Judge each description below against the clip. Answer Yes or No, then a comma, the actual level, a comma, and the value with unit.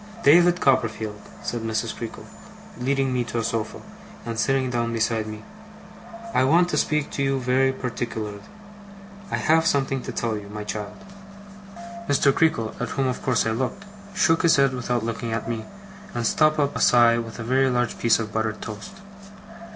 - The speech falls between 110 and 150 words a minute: No, average, 180 wpm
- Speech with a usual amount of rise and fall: Yes, average, 3.2 semitones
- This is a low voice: Yes, low, 120 Hz